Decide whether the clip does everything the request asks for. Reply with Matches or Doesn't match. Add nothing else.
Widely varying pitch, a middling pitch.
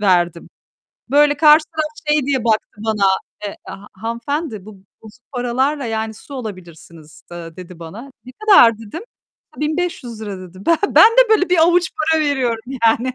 Doesn't match